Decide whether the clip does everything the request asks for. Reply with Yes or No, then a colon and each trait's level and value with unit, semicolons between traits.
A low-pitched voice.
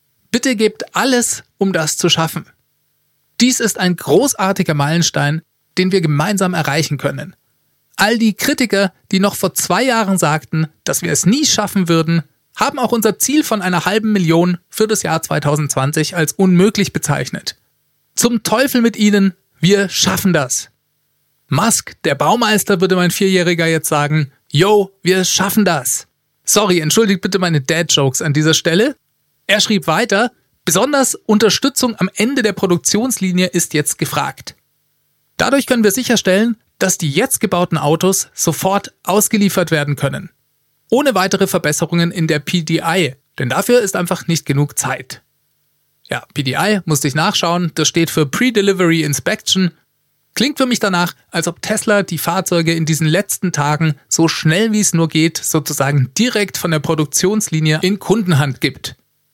No: medium, 175 Hz